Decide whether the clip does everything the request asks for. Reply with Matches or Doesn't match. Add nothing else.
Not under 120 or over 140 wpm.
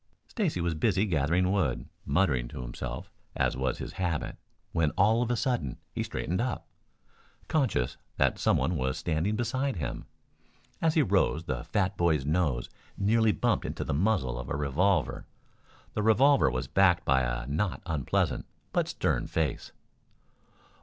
Doesn't match